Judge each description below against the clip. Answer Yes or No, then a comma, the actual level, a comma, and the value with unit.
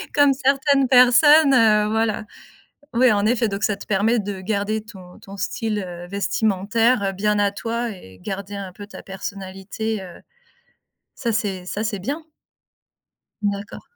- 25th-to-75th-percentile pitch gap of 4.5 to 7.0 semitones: No, average, 2.8 semitones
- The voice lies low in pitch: No, high, 210 Hz